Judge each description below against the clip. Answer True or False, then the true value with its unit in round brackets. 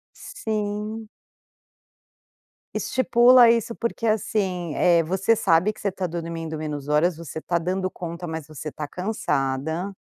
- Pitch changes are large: False (4.9 semitones)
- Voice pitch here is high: False (180 Hz)